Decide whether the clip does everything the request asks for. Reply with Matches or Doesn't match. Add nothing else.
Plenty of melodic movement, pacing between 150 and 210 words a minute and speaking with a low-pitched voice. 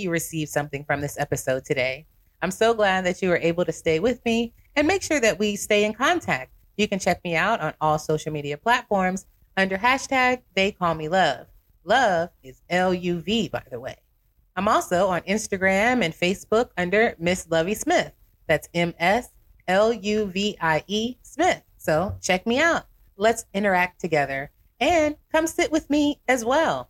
Doesn't match